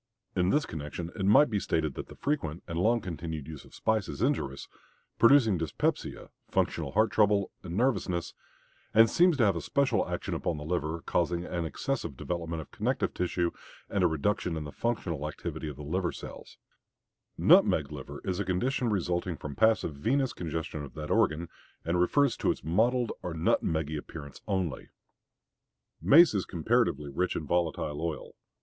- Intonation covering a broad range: Yes, wide, 5.7 semitones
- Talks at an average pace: Yes, average, 175 wpm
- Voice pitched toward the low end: Yes, very low, 85 Hz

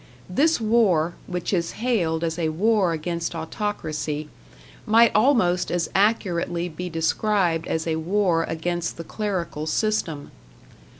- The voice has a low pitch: No, medium, 175 Hz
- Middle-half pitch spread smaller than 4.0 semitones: No, average, 4.3 semitones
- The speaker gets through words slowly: Yes, slow, 125 wpm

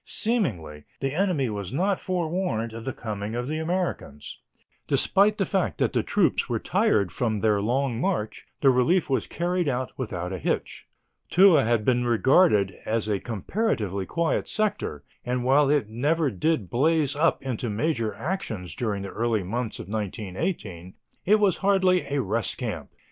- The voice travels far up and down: Yes, wide, 8.0 semitones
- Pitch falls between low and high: No, low, 125 Hz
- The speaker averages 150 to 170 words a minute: Yes, average, 165 wpm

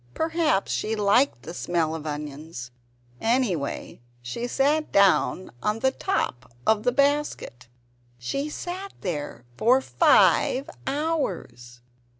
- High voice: Yes, high, 210 Hz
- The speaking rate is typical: No, slow, 115 wpm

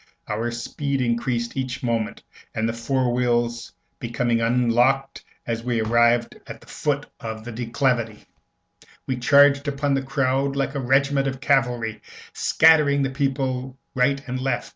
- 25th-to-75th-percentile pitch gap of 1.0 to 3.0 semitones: Yes, narrow, 2.5 semitones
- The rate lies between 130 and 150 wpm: Yes, average, 145 wpm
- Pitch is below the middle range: Yes, low, 125 Hz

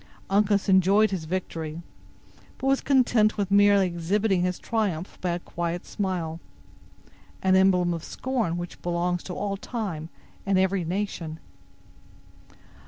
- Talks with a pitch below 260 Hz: Yes, medium, 185 Hz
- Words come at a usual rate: No, slow, 125 wpm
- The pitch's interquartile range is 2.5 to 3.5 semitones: Yes, average, 2.8 semitones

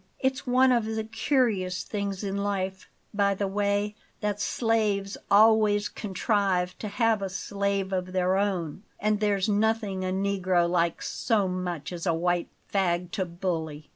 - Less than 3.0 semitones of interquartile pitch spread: Yes, narrow, 2.4 semitones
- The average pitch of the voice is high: Yes, high, 200 Hz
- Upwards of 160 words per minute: No, average, 155 wpm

